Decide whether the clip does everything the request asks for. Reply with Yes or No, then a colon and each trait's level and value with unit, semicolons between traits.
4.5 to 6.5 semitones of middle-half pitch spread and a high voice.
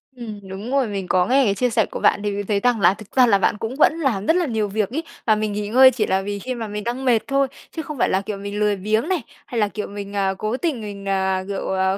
No: average, 3.8 semitones; high, 210 Hz